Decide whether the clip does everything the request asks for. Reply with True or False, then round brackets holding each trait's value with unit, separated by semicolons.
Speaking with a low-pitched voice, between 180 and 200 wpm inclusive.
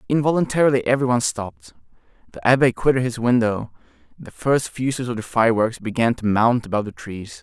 False (120 Hz; 170 wpm)